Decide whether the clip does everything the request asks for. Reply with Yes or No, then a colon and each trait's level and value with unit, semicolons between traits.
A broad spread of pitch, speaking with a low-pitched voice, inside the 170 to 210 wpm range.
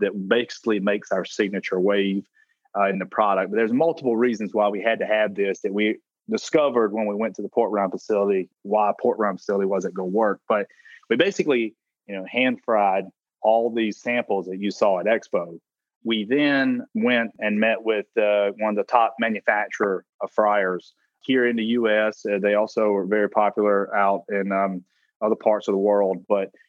No: narrow, 2.4 semitones; low, 105 Hz; average, 195 wpm